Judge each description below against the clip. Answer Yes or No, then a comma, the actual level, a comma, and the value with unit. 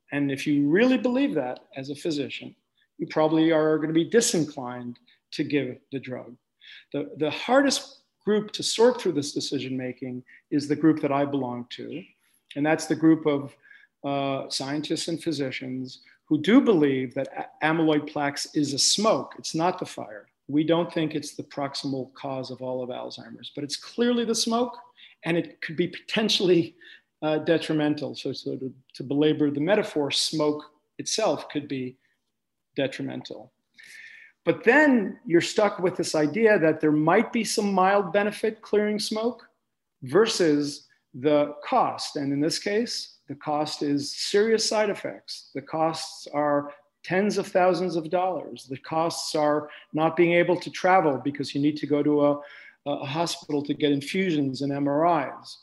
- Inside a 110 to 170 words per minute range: Yes, average, 165 wpm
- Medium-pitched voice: Yes, medium, 155 Hz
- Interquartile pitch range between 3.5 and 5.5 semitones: Yes, average, 4.7 semitones